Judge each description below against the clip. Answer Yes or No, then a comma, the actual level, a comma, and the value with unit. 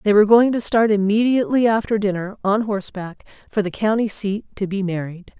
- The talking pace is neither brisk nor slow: Yes, average, 190 wpm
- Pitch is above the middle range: Yes, high, 205 Hz